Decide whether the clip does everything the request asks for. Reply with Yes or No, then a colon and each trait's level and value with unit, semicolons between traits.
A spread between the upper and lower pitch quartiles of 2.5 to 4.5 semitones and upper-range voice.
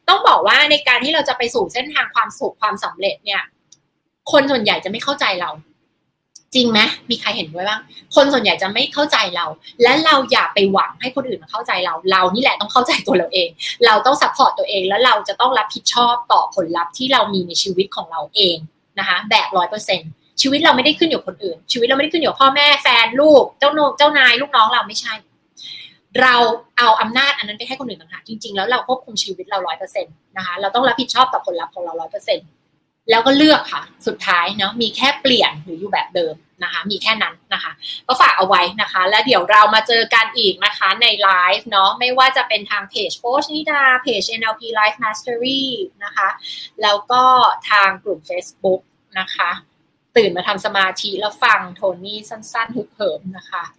No: average, 5.3 semitones; high, 220 Hz